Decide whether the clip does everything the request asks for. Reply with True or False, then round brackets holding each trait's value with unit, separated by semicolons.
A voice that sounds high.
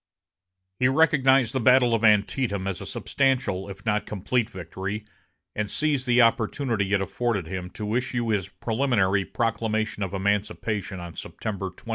False (110 Hz)